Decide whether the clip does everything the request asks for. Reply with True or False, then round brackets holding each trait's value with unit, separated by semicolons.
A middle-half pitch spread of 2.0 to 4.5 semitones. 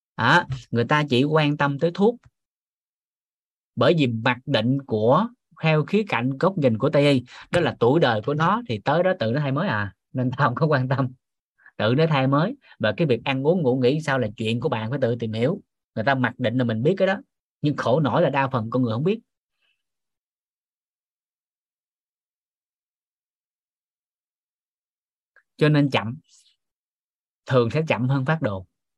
True (4.2 semitones)